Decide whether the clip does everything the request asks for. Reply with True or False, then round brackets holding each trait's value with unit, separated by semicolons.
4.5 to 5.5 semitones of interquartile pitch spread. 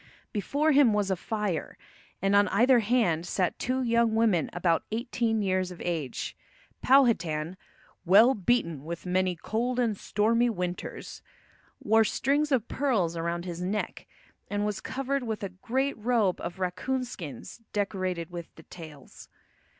True (5.2 semitones)